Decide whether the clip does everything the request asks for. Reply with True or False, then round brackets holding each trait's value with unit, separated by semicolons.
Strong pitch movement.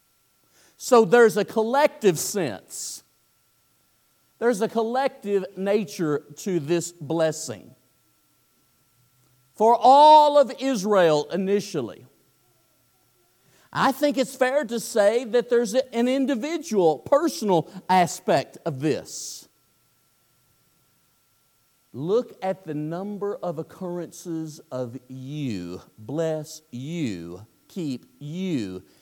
True (9.0 semitones)